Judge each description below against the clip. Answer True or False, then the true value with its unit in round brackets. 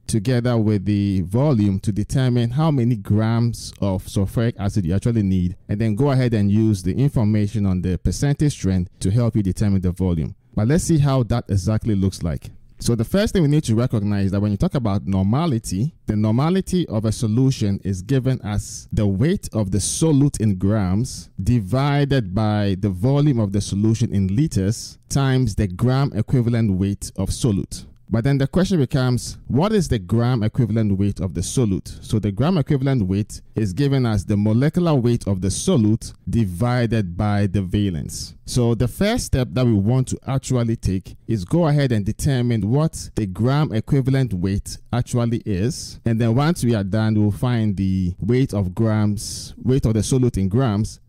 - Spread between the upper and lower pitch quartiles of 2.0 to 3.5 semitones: False (4.1 semitones)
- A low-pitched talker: True (110 Hz)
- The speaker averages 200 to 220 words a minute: False (190 wpm)